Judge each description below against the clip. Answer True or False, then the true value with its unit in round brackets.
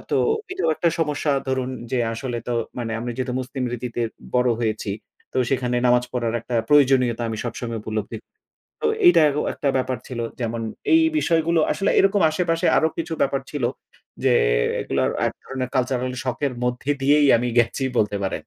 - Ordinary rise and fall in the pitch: True (3.4 semitones)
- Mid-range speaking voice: False (125 Hz)